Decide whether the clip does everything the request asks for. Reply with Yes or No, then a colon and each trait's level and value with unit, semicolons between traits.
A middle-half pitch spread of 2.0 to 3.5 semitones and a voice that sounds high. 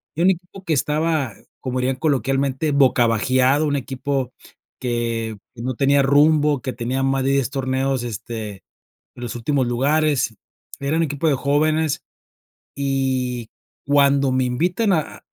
No: average, 2.8 semitones; low, 135 Hz